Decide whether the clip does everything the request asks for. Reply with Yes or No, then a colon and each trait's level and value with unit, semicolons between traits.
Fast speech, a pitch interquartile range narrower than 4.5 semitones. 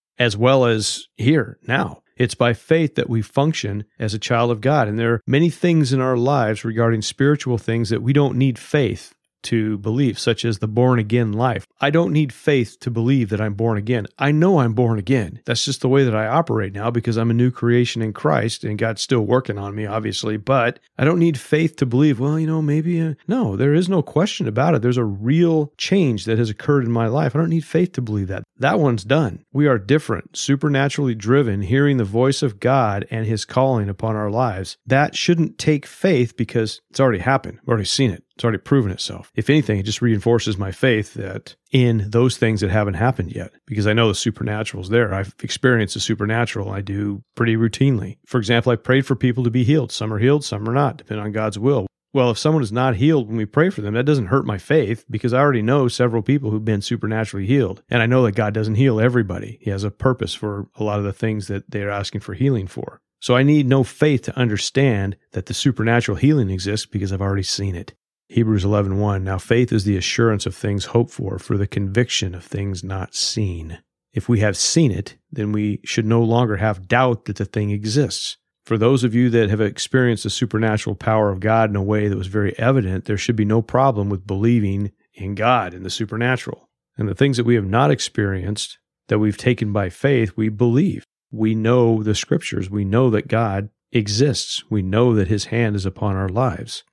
Yes: fast, 225 wpm; average, 3.9 semitones